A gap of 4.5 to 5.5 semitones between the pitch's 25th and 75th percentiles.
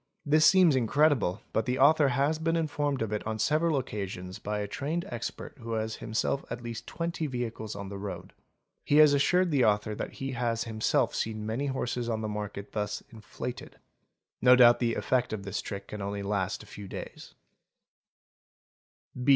Yes: average, 5.0 semitones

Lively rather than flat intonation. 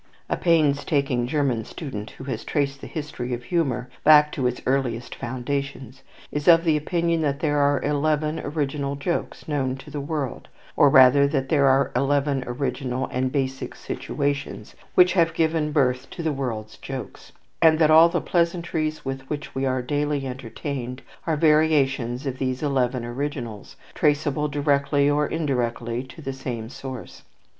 No: average, 2.7 semitones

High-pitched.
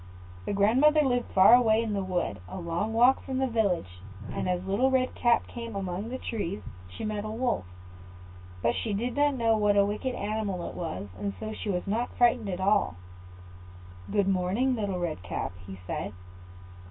Yes: high, 210 Hz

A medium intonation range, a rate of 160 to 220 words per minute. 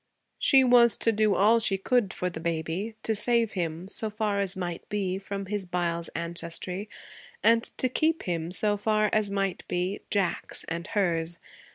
Yes: average, 3.7 semitones; average, 175 wpm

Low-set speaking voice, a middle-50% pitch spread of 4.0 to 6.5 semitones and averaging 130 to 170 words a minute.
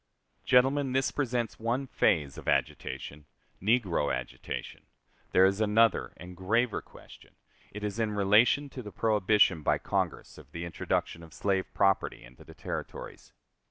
Yes: low, 105 Hz; average, 4.7 semitones; average, 145 wpm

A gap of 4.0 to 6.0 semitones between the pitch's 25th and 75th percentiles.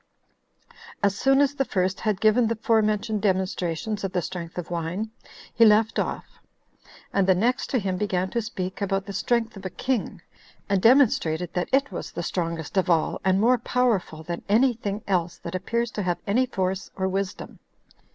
No: average, 3.6 semitones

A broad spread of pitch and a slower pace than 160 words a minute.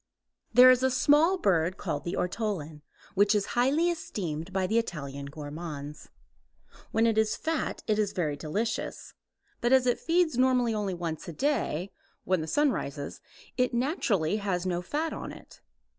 No: wide, 7.5 semitones; average, 165 wpm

